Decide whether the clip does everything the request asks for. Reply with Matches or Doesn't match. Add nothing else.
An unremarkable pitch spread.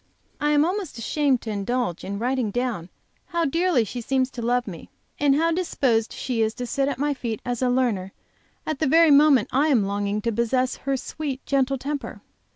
Matches